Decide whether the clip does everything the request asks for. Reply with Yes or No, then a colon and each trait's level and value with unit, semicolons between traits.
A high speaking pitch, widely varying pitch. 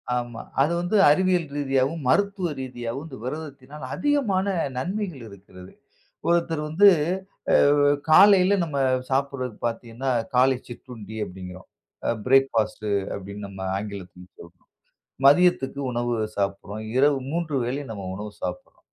No: low, 130 Hz; wide, 7.1 semitones